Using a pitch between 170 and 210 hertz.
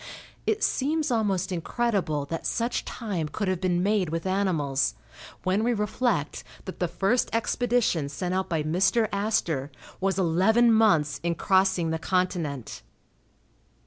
Yes: high, 190 Hz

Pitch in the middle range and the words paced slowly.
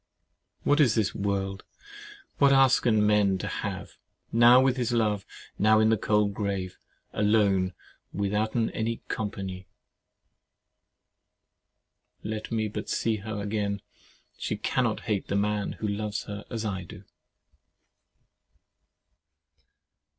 No: low, 105 Hz; slow, 115 wpm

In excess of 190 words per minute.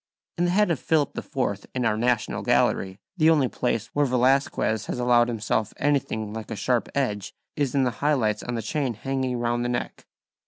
Yes: average, 200 wpm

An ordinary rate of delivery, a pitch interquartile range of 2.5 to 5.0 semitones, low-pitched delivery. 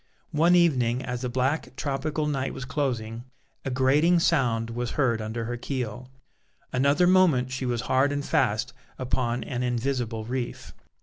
Yes: average, 150 wpm; average, 2.9 semitones; low, 130 Hz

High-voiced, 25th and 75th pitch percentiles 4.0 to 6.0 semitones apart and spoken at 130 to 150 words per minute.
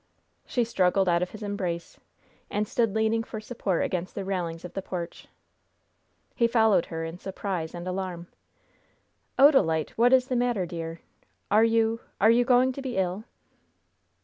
No: high, 200 Hz; average, 4.5 semitones; average, 160 wpm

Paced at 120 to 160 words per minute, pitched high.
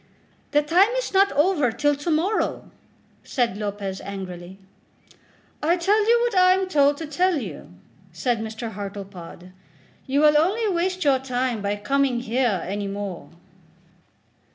Yes: average, 145 wpm; very high, 265 Hz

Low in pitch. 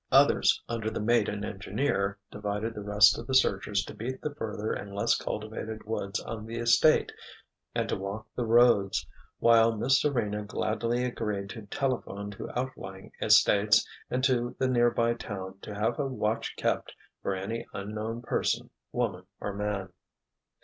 Yes: low, 110 Hz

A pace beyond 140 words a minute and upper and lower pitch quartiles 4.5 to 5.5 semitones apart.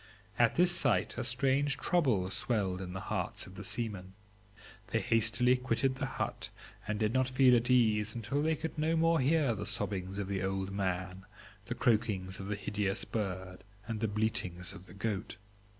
Yes: average, 180 wpm; average, 4.9 semitones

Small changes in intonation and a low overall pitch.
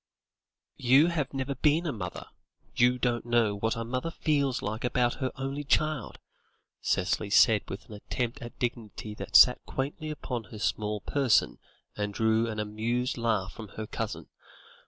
No: average, 3.7 semitones; low, 120 Hz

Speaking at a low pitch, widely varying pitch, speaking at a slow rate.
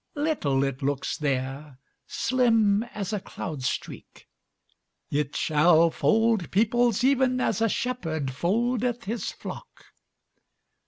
No: high, 200 Hz; wide, 8.5 semitones; slow, 90 wpm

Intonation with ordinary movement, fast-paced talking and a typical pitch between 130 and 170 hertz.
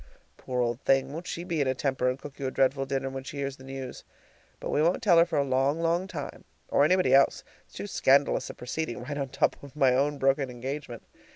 No: narrow, 2.2 semitones; fast, 245 wpm; low, 135 Hz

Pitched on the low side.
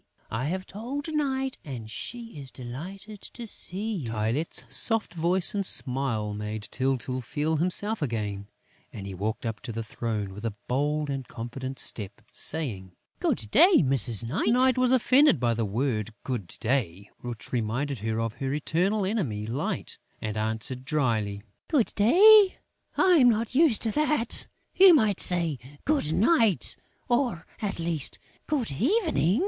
No: medium, 145 Hz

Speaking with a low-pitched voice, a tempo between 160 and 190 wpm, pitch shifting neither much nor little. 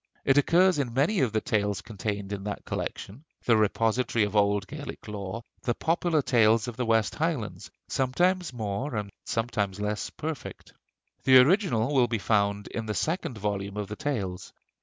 Yes: low, 115 Hz; average, 170 wpm; average, 4.8 semitones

